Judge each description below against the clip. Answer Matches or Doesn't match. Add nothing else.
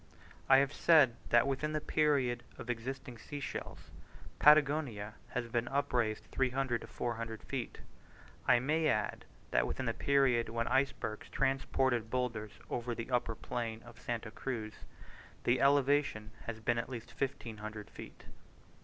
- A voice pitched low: Matches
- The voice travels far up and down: Doesn't match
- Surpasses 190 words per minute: Doesn't match